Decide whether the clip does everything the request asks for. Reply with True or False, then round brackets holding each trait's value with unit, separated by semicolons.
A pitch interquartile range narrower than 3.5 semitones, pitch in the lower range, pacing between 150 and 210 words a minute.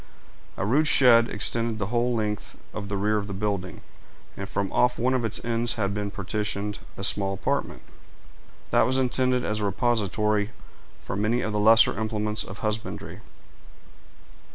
True (2.5 semitones; 105 Hz; 165 wpm)